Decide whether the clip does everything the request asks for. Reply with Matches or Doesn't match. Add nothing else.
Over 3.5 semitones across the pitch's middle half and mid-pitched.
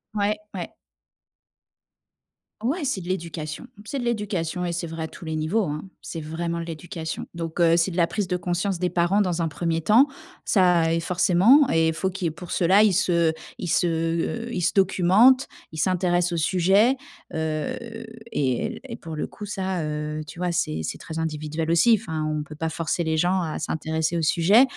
Doesn't match